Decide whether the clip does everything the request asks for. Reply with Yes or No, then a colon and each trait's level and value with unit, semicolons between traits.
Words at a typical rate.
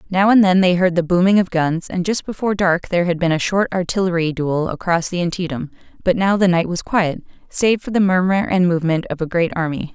No: fast, 235 wpm